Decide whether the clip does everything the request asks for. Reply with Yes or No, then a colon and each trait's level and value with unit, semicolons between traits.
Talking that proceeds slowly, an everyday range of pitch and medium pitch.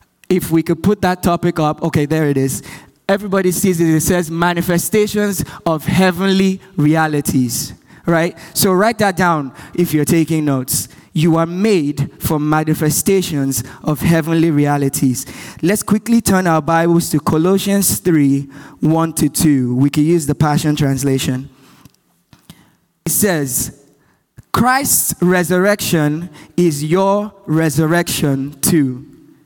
Yes: slow, 125 wpm; average, 3.5 semitones; medium, 165 Hz